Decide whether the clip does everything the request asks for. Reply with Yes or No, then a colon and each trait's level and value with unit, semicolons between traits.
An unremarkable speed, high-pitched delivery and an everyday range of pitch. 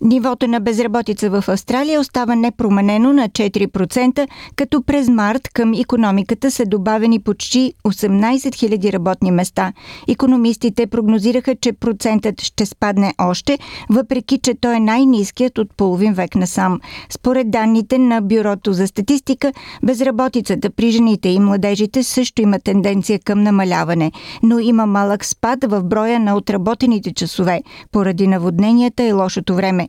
Yes: average, 135 wpm; high, 225 Hz; average, 3.7 semitones